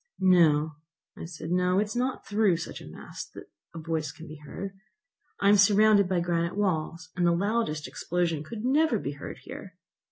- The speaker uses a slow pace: No, average, 190 wpm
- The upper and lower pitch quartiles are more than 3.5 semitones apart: Yes, average, 4.2 semitones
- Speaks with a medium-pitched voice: Yes, medium, 175 Hz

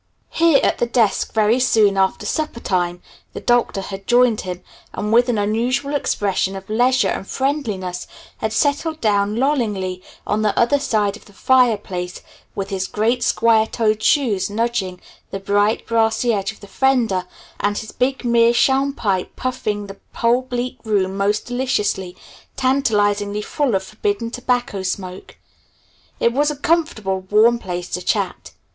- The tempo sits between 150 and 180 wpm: Yes, average, 155 wpm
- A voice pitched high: Yes, high, 220 Hz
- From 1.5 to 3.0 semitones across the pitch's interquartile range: No, average, 3.9 semitones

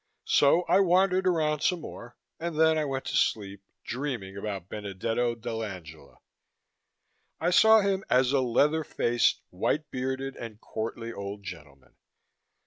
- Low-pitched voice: Yes, low, 125 Hz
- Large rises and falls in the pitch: Yes, wide, 7.3 semitones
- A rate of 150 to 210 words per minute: No, slow, 135 wpm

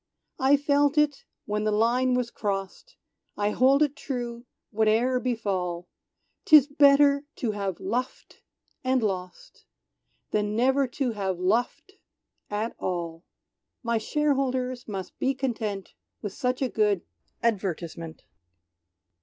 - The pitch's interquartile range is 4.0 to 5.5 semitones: Yes, average, 4.6 semitones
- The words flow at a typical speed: No, slow, 120 wpm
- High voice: Yes, high, 235 Hz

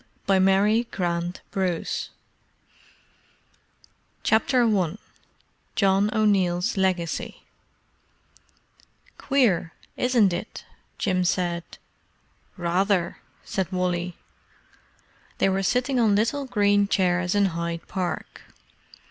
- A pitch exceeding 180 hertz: Yes, high, 190 Hz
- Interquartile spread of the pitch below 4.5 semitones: Yes, average, 2.9 semitones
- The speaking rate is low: Yes, slow, 85 wpm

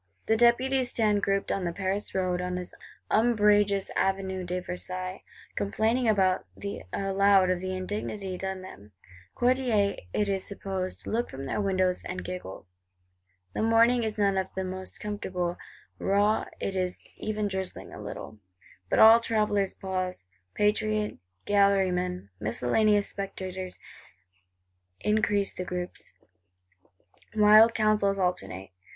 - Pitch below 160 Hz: No, high, 195 Hz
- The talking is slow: Yes, slow, 125 wpm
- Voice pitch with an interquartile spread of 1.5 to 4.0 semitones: Yes, narrow, 2.4 semitones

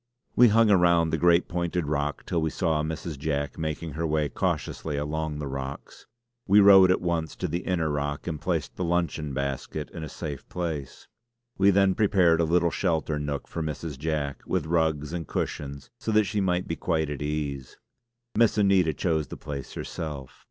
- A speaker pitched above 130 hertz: No, very low, 80 Hz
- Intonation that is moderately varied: Yes, average, 3.1 semitones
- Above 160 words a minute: Yes, average, 185 wpm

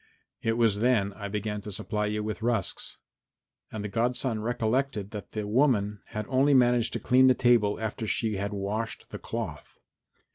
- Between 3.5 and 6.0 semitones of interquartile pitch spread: No, average, 2.7 semitones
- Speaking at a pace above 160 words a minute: Yes, average, 175 wpm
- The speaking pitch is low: Yes, low, 110 Hz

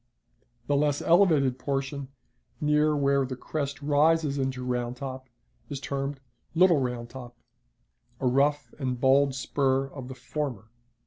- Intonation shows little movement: Yes, narrow, 2.0 semitones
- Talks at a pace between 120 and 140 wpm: Yes, slow, 135 wpm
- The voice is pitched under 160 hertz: Yes, low, 135 Hz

